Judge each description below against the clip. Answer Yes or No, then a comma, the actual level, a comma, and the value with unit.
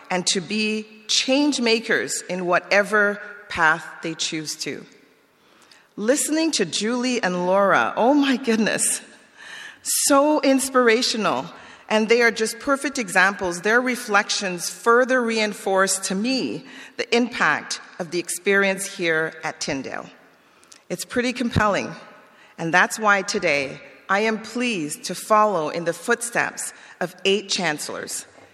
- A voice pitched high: Yes, high, 210 Hz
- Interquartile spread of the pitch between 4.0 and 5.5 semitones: Yes, average, 4.5 semitones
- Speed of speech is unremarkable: No, slow, 125 wpm